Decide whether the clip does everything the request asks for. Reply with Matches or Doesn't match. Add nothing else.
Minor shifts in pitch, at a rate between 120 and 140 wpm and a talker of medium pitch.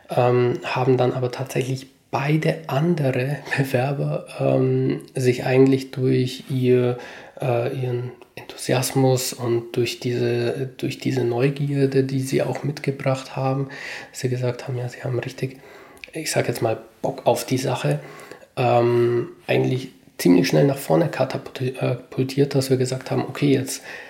Doesn't match